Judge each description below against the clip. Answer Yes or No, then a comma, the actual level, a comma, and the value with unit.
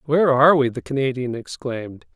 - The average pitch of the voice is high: No, low, 135 Hz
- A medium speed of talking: Yes, average, 165 wpm